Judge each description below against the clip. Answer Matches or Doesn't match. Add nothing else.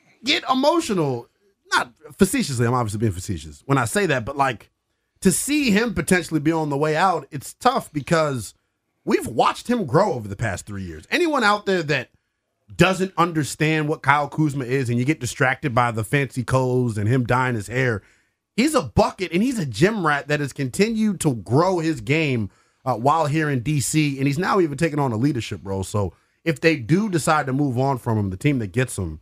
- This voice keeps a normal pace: Doesn't match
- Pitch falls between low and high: Matches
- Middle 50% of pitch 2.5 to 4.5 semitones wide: Doesn't match